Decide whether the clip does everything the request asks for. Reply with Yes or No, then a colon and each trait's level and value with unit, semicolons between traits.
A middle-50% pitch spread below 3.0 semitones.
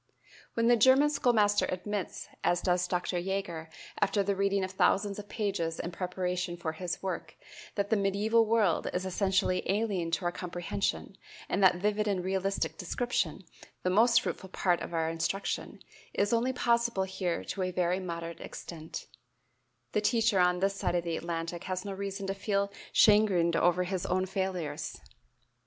Yes: narrow, 2.5 semitones